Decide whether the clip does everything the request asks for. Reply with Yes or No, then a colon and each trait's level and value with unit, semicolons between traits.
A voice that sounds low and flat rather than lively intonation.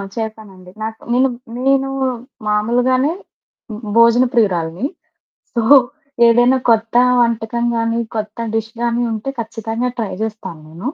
No: high, 225 Hz; narrow, 2.0 semitones